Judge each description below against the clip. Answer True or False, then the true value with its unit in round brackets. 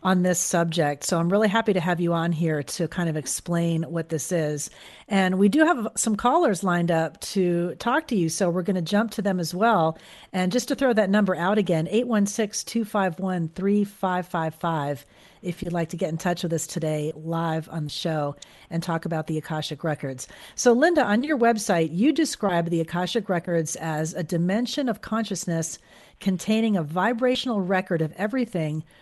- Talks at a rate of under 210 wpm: True (190 wpm)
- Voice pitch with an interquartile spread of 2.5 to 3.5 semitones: False (4.2 semitones)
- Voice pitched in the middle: True (180 Hz)